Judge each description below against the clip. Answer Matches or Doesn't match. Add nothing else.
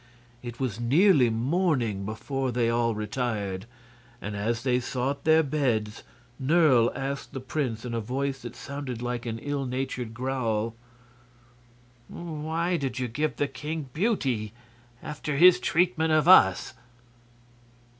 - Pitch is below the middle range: Matches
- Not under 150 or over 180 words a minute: Doesn't match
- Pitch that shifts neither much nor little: Matches